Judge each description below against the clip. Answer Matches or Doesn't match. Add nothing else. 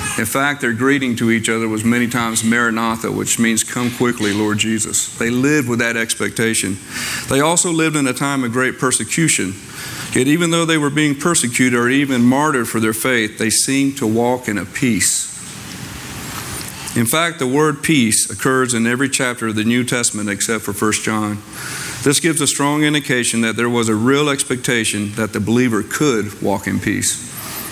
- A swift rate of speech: Doesn't match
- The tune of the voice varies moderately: Matches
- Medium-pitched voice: Doesn't match